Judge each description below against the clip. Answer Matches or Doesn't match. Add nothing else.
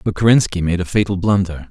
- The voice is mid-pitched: Doesn't match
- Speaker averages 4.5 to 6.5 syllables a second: Matches